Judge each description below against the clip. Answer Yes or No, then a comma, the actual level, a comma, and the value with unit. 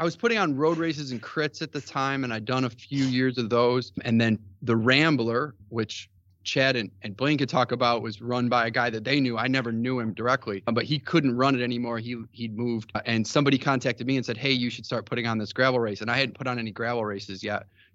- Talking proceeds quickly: Yes, fast, 255 wpm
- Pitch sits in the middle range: No, low, 120 Hz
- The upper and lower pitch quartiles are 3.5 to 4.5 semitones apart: No, average, 2.8 semitones